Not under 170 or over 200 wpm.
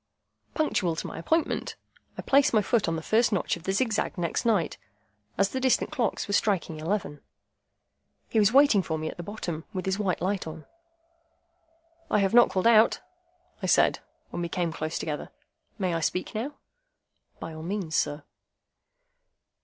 Yes: average, 175 wpm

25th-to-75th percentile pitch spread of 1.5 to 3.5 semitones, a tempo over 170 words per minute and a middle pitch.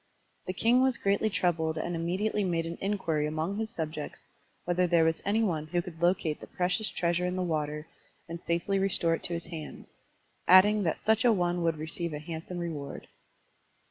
Yes: average, 2.9 semitones; average, 195 wpm; medium, 175 Hz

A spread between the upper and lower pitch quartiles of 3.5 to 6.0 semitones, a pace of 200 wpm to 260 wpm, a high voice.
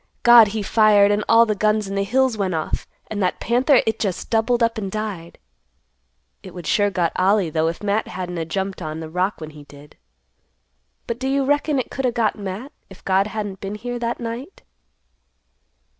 Yes: average, 3.9 semitones; fast, 205 wpm; high, 205 Hz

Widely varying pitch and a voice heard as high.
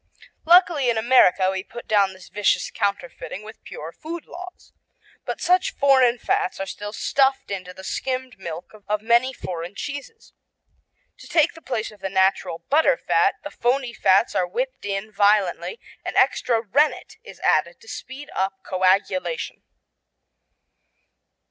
Yes: wide, 6.2 semitones; high, 220 Hz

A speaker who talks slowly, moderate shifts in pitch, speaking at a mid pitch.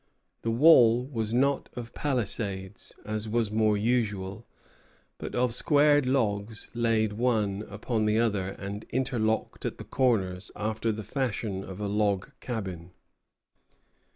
No: slow, 125 wpm; average, 3.0 semitones; low, 110 Hz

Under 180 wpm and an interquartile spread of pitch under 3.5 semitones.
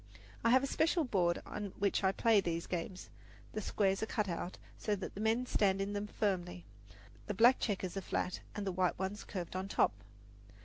No: fast, 205 wpm; narrow, 2.5 semitones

